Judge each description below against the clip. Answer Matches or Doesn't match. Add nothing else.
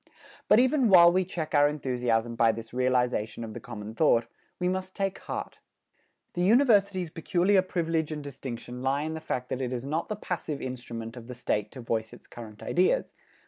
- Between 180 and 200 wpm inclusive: Matches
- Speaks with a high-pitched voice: Doesn't match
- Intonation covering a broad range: Matches